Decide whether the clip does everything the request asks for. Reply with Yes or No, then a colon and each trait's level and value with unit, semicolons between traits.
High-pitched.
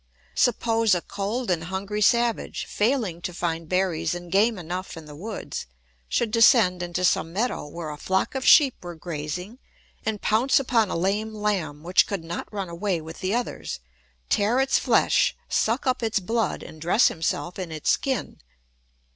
Yes: high, 195 Hz